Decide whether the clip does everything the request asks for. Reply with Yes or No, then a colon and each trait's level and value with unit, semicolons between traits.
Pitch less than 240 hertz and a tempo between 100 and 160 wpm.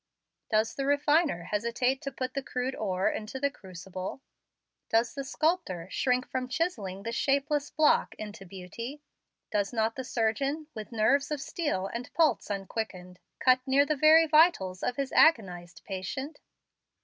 No: very high, 250 Hz; average, 150 wpm